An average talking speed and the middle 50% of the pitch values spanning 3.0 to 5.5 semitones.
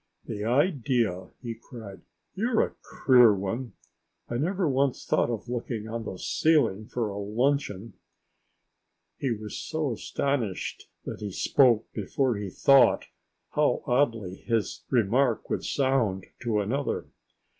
No: slow, 130 wpm; average, 4.4 semitones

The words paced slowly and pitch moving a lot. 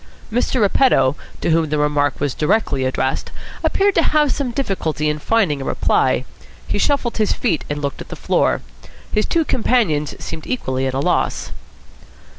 No: average, 170 wpm; wide, 9.0 semitones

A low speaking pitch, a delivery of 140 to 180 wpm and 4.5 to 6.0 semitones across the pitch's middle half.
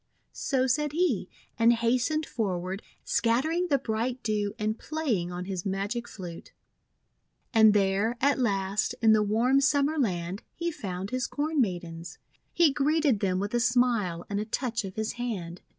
No: high, 225 Hz; average, 160 wpm; average, 5.1 semitones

